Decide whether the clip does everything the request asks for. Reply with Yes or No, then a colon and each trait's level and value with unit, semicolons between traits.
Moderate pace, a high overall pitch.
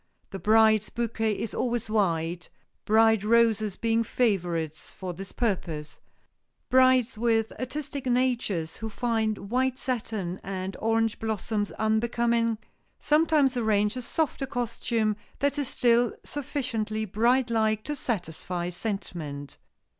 No: slow, 115 wpm; high, 225 Hz